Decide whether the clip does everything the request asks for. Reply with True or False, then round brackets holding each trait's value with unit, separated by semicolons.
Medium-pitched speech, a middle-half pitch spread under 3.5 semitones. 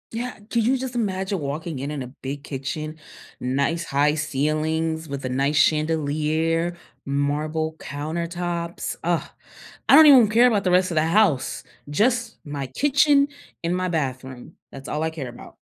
False (160 Hz; 4.3 semitones)